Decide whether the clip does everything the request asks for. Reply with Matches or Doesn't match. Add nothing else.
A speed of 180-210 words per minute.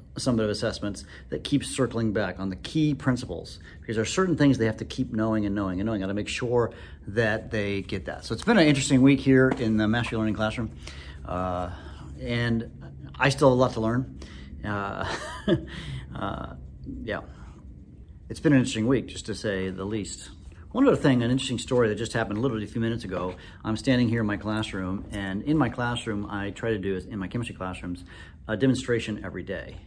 Matches